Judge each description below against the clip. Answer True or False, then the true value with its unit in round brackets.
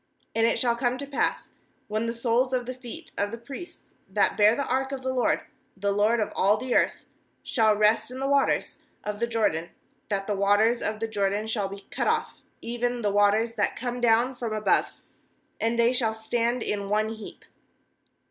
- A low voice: False (225 Hz)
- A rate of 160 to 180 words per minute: False (200 wpm)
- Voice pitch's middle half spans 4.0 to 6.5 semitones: False (2.7 semitones)